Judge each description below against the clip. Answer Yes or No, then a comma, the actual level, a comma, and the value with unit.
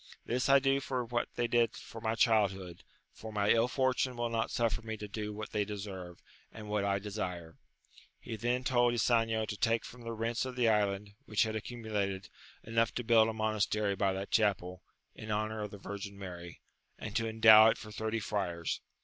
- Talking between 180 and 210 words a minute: Yes, average, 200 wpm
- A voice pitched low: Yes, low, 110 Hz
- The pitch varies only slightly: Yes, narrow, 2.3 semitones